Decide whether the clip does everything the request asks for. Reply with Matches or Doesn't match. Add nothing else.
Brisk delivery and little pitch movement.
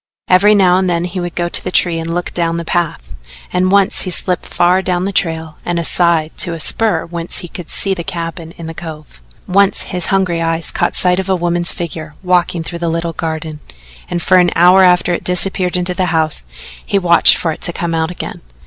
Matches